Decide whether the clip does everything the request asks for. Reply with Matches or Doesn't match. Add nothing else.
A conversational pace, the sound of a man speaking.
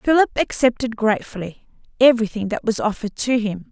Doesn't match